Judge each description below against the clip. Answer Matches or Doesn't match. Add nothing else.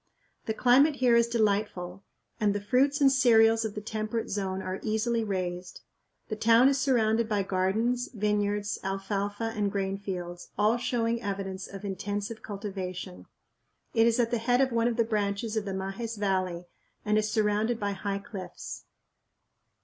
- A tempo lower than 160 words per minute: Doesn't match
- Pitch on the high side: Matches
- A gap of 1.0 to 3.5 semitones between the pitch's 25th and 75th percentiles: Matches